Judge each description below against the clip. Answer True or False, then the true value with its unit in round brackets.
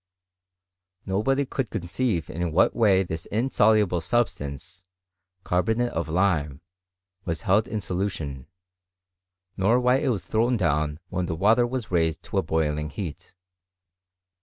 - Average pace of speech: False (130 wpm)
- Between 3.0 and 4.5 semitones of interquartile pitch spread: False (5.6 semitones)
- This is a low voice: True (95 Hz)